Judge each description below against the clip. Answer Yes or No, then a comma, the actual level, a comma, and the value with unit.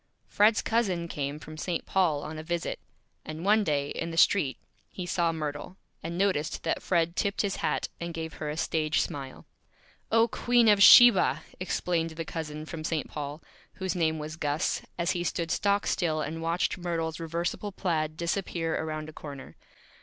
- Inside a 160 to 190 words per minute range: Yes, average, 175 wpm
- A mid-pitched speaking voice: Yes, medium, 165 Hz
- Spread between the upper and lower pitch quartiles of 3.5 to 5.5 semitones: No, average, 2.7 semitones